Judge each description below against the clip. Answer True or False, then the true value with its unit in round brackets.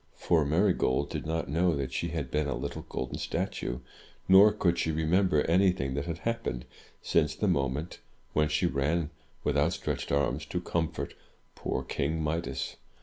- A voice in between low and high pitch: False (80 Hz)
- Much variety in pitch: False (3.4 semitones)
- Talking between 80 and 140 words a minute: False (175 wpm)